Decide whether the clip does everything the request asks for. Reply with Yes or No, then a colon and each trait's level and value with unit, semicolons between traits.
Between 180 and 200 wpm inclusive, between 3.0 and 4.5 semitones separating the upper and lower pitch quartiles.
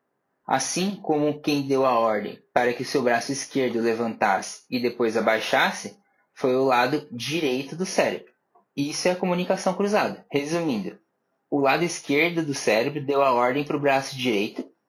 No: average, 160 wpm; average, 4.2 semitones